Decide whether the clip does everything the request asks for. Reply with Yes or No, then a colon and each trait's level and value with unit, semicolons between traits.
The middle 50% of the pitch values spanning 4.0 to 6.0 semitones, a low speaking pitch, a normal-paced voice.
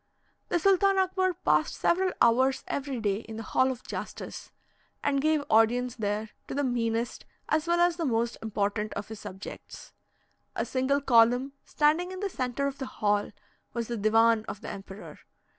No: average, 5.1 semitones; very high, 250 Hz; average, 175 wpm